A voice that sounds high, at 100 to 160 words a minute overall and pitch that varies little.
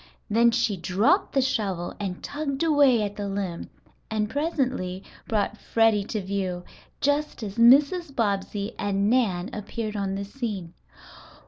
No: high, 215 Hz; average, 140 wpm; average, 4.7 semitones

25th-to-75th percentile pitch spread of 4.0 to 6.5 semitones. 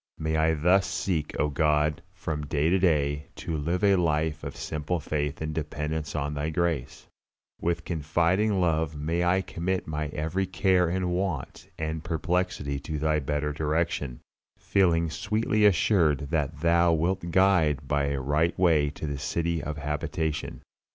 No: average, 2.7 semitones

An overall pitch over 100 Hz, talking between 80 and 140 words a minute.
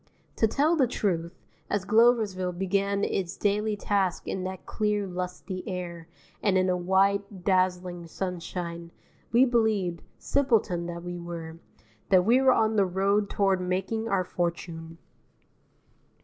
Yes: high, 190 Hz; slow, 135 wpm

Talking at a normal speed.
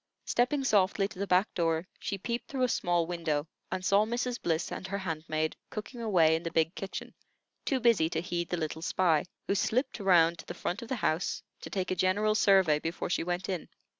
No: fast, 215 wpm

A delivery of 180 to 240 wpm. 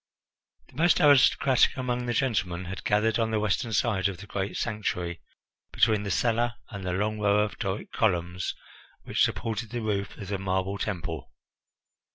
No: average, 170 wpm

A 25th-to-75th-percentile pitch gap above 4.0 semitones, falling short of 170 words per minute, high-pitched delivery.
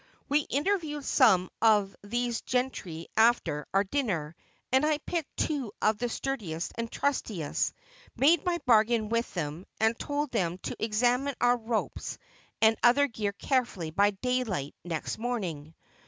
Yes: average, 5.3 semitones; average, 140 wpm; high, 230 Hz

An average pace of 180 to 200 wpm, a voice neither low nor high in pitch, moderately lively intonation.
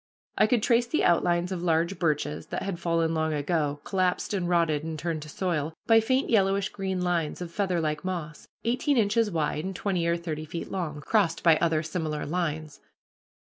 Yes: average, 185 wpm; medium, 170 Hz; average, 3.5 semitones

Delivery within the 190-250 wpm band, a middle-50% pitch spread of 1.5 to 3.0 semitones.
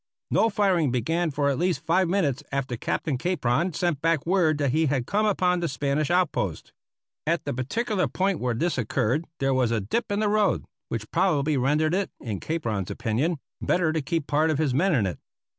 No: average, 200 wpm; average, 5.2 semitones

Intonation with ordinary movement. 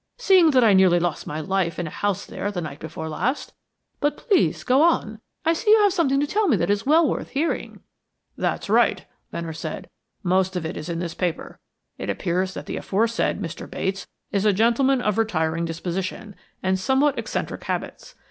No: wide, 7.3 semitones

